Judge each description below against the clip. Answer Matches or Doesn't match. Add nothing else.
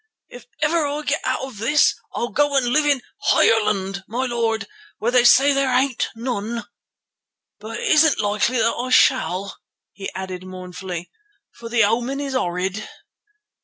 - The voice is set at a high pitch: Matches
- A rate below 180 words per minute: Matches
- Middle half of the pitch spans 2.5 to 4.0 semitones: Doesn't match